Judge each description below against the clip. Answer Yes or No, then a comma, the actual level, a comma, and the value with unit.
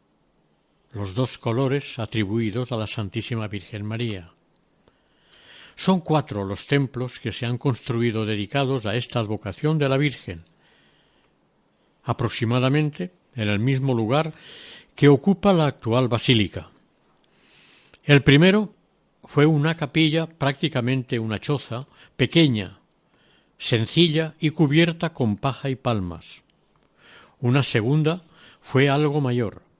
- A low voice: Yes, low, 130 Hz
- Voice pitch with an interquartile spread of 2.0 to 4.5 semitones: No, average, 5.0 semitones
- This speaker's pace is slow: Yes, slow, 110 wpm